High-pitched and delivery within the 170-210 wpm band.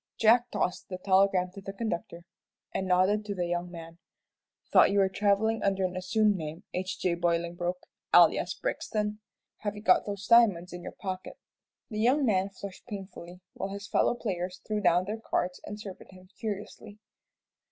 Yes: high, 195 Hz; average, 175 wpm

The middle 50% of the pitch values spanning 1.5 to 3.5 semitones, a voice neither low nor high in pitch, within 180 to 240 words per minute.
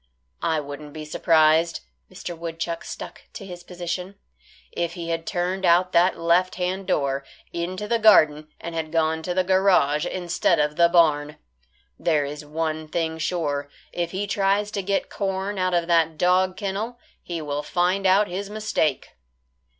No: average, 2.9 semitones; medium, 170 Hz; average, 165 wpm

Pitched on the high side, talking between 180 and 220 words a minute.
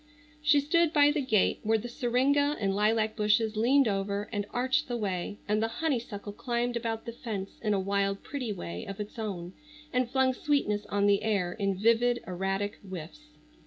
Yes: high, 220 Hz; average, 185 wpm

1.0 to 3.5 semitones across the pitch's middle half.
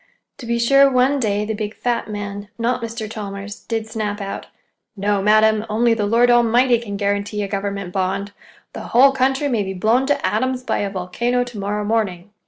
Yes: average, 3.0 semitones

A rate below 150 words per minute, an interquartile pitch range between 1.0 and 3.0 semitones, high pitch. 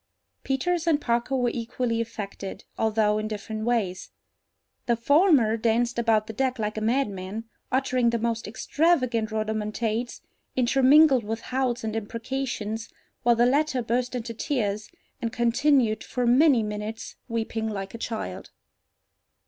Yes: slow, 135 wpm; average, 2.7 semitones; high, 230 Hz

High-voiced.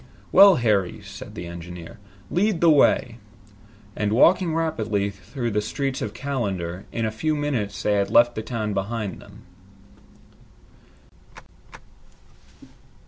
No: low, 110 Hz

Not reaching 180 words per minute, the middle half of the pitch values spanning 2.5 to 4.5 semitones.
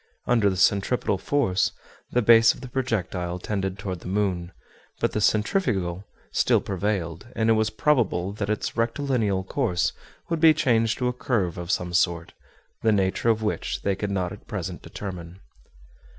Yes: average, 165 wpm; average, 3.9 semitones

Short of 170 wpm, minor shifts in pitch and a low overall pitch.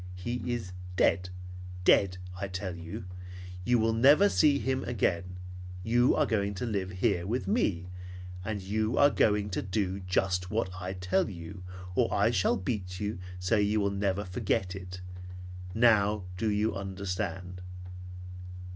No: average, 150 wpm; average, 3.2 semitones; low, 100 Hz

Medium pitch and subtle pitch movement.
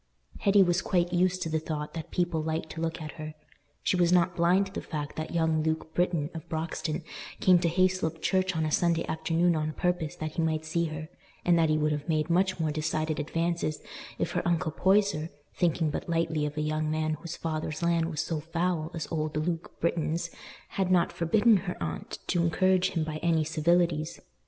Yes: medium, 165 Hz; narrow, 2.0 semitones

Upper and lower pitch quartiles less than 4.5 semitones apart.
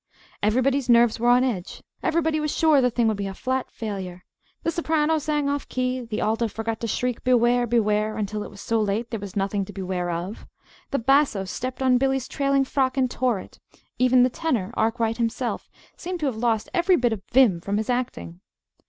Yes: average, 3.9 semitones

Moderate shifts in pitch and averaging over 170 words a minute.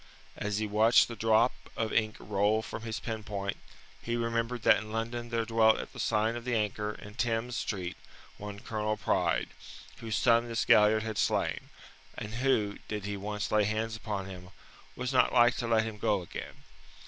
No: narrow, 1.7 semitones; average, 190 wpm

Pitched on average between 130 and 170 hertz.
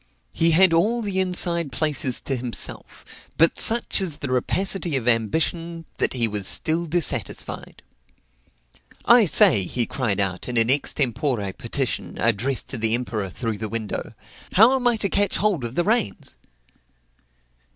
Yes: medium, 140 Hz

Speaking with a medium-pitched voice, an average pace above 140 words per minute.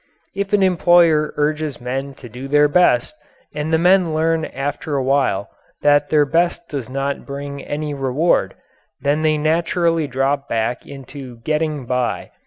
Yes: medium, 145 Hz; average, 155 wpm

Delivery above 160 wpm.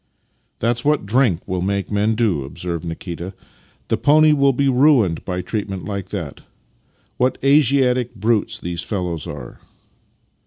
No: average, 150 wpm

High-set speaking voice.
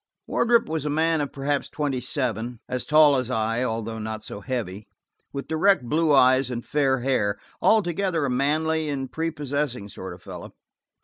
No: low, 135 Hz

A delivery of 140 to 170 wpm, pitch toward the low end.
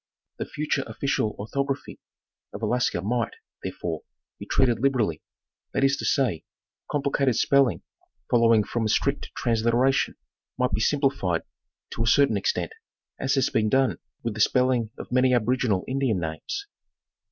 Yes: average, 145 wpm; low, 125 Hz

